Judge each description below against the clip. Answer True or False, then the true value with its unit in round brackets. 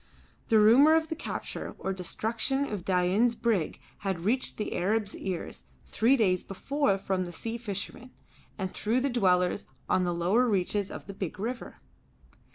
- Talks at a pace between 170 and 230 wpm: False (160 wpm)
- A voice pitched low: False (210 Hz)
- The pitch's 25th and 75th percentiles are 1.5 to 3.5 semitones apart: False (4.3 semitones)